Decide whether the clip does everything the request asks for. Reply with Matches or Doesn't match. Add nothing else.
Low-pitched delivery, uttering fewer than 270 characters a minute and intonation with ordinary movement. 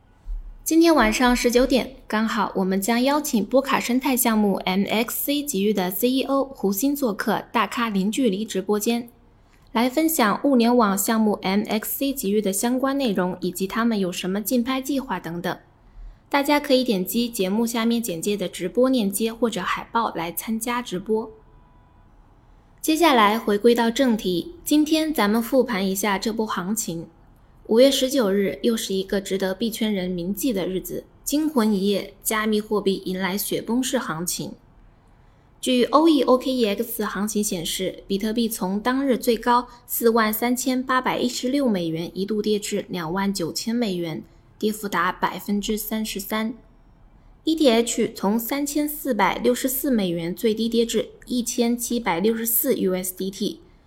Doesn't match